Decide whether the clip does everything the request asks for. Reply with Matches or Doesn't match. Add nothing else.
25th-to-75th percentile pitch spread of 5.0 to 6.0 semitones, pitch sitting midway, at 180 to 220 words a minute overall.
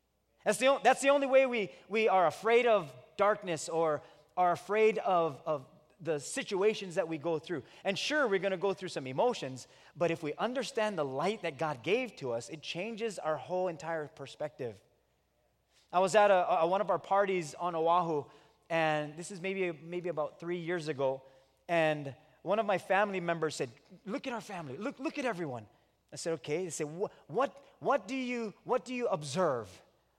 Matches